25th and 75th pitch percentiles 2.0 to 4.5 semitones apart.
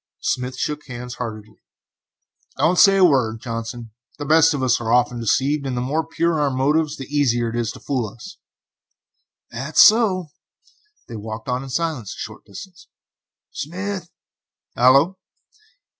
No: average, 5.1 semitones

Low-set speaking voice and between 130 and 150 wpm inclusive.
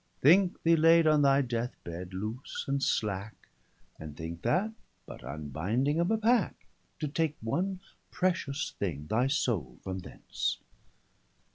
Yes: low, 130 Hz; average, 140 wpm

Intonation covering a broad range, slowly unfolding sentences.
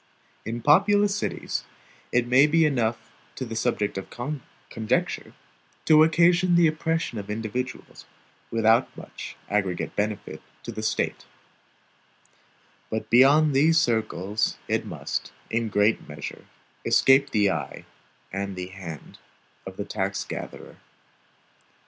Yes: wide, 6.7 semitones; slow, 120 wpm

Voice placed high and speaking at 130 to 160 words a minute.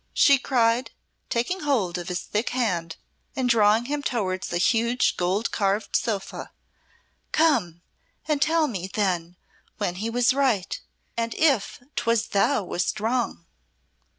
Yes: high, 230 Hz; slow, 135 wpm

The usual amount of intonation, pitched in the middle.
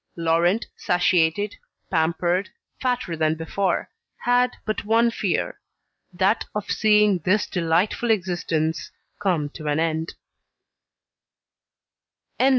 Yes: average, 4.4 semitones; medium, 180 Hz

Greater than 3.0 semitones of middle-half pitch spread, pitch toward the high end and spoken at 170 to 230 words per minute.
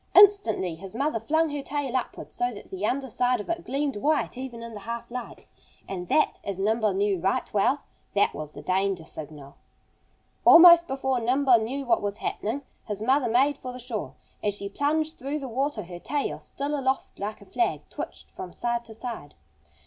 Yes: wide, 5.5 semitones; high, 240 Hz; average, 195 wpm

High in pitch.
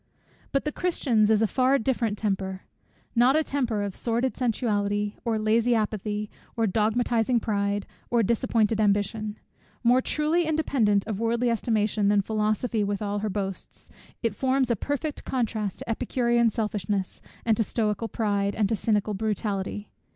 Yes: high, 220 Hz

